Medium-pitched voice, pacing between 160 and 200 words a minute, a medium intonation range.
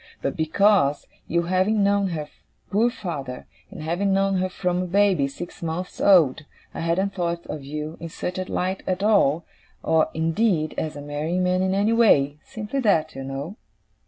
Yes: medium, 175 Hz; average, 180 wpm; average, 4.1 semitones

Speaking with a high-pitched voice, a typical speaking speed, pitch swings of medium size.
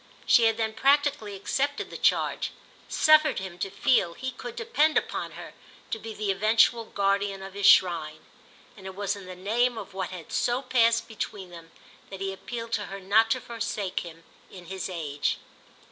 Yes: high, 205 Hz; average, 185 wpm; average, 3.7 semitones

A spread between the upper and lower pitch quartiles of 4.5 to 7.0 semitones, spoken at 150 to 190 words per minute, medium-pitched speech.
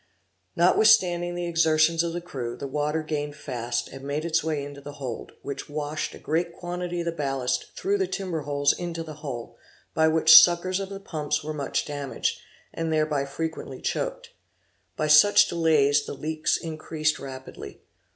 No: average, 3.0 semitones; average, 175 wpm; medium, 155 Hz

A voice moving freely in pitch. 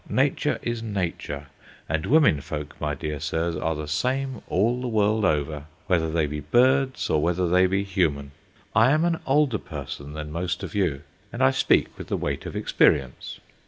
Yes: wide, 7.7 semitones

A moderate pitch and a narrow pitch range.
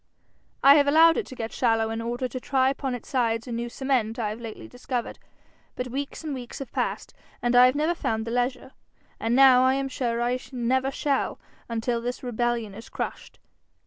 No: high, 245 Hz; narrow, 2.3 semitones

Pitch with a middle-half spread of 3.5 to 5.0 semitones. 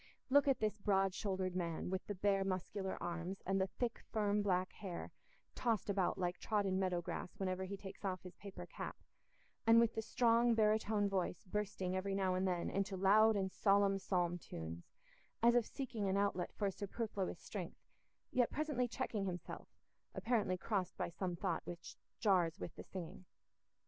No: narrow, 2.4 semitones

